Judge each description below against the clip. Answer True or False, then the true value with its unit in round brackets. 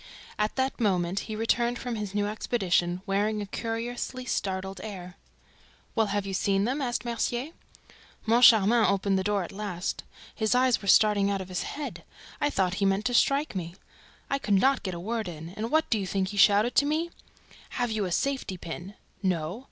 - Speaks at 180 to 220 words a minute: True (195 wpm)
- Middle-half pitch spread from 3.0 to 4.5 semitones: True (3.9 semitones)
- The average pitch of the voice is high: True (210 Hz)